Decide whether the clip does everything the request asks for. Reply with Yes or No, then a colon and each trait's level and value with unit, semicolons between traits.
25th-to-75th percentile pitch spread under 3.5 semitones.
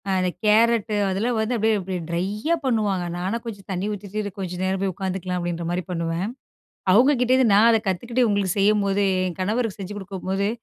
Yes: average, 2.9 semitones